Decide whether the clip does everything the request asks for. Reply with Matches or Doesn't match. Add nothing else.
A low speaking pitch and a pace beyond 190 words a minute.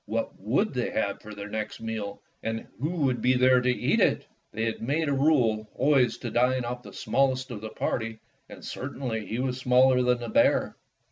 Matches